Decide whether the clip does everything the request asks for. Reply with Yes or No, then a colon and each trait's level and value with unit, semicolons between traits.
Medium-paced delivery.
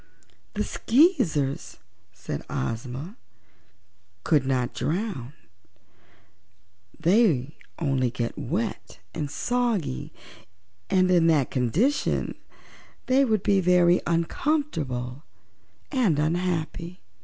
No: slow, 85 wpm